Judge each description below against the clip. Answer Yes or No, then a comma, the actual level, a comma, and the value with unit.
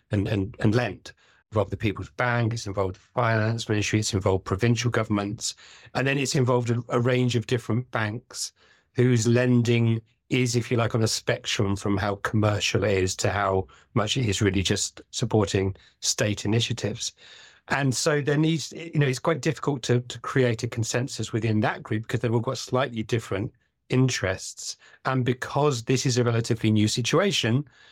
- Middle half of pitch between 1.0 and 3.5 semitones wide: Yes, average, 3.1 semitones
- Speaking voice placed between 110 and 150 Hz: Yes, low, 120 Hz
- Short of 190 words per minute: Yes, average, 180 wpm